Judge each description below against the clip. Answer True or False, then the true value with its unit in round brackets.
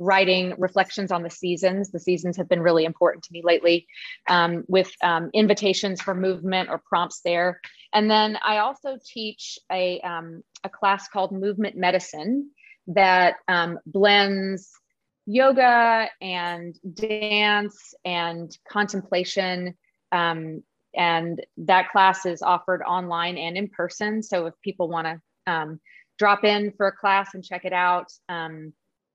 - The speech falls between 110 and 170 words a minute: True (140 wpm)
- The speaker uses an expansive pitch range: False (2.7 semitones)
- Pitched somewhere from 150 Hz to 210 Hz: True (185 Hz)